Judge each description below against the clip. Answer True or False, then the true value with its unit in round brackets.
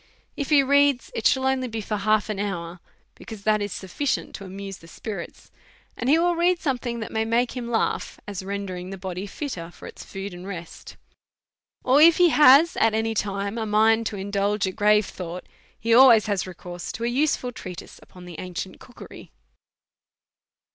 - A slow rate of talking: False (190 wpm)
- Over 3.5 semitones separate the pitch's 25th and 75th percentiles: True (4.4 semitones)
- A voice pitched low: False (215 Hz)